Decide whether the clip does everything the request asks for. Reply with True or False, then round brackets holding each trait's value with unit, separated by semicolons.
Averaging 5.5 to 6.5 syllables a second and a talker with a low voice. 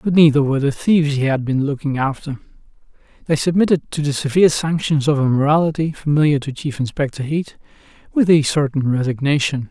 False (6.0 syllables/s; 145 Hz)